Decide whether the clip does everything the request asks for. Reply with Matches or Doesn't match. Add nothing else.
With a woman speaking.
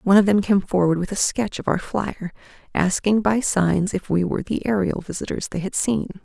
Matches